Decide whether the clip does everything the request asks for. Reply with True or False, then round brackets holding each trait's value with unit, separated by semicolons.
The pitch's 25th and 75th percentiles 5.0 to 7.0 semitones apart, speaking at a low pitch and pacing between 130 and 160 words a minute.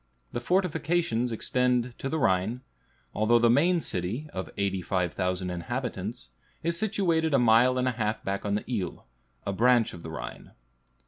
True (5.4 semitones; 120 Hz; 155 wpm)